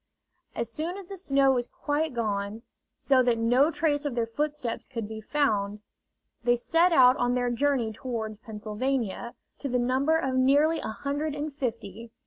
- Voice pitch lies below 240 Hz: No, very high, 255 Hz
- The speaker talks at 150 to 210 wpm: Yes, average, 170 wpm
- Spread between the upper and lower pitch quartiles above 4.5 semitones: No, average, 4.2 semitones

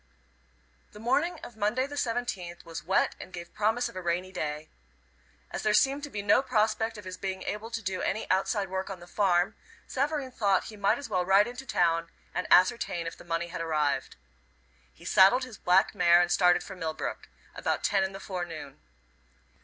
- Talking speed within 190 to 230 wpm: Yes, average, 195 wpm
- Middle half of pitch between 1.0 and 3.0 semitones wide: No, average, 4.1 semitones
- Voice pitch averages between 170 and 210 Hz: Yes, high, 190 Hz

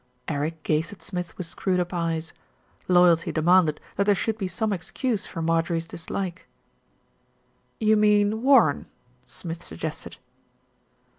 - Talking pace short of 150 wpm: Yes, slow, 135 wpm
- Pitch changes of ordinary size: Yes, average, 3.7 semitones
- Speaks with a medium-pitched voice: Yes, medium, 180 Hz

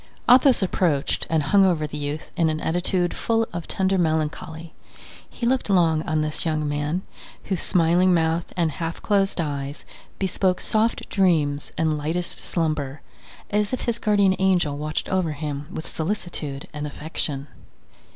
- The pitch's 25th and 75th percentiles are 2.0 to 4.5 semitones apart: Yes, average, 3.7 semitones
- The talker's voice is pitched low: No, medium, 165 Hz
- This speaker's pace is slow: No, average, 150 wpm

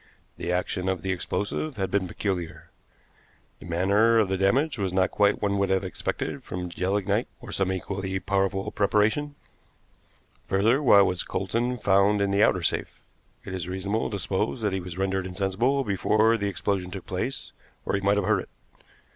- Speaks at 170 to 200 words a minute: Yes, average, 180 wpm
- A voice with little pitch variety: Yes, narrow, 2.0 semitones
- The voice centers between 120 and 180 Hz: No, very low, 95 Hz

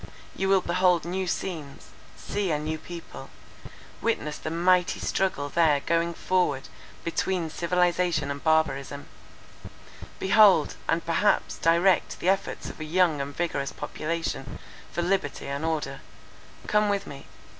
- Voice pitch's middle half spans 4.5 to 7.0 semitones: No, average, 3.6 semitones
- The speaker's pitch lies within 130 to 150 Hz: No, medium, 170 Hz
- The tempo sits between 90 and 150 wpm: Yes, slow, 135 wpm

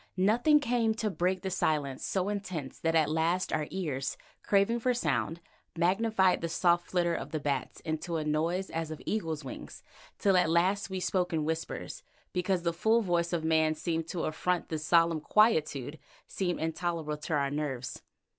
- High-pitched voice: No, medium, 170 Hz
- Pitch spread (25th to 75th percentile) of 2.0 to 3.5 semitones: Yes, average, 3.2 semitones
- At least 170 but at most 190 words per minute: Yes, average, 175 wpm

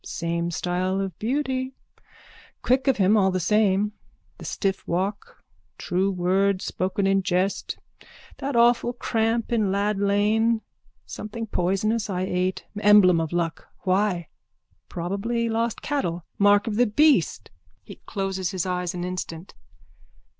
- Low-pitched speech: No, high, 195 Hz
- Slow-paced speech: Yes, slow, 130 wpm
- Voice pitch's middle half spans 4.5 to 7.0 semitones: No, average, 3.4 semitones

